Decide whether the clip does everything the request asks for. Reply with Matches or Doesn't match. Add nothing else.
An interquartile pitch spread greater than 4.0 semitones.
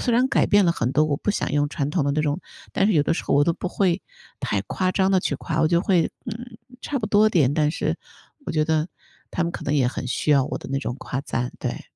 Matches